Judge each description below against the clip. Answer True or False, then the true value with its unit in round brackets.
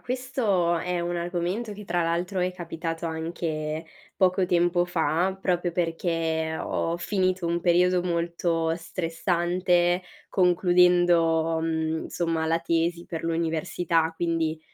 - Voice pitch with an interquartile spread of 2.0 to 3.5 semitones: False (1.4 semitones)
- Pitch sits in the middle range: True (170 Hz)